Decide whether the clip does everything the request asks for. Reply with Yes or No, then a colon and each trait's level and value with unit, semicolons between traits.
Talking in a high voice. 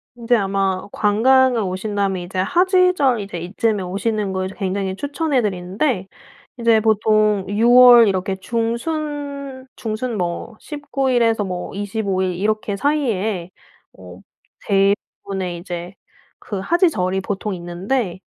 Yes: high, 210 Hz